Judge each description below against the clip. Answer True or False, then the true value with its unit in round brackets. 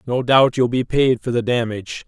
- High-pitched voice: False (125 Hz)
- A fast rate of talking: True (230 wpm)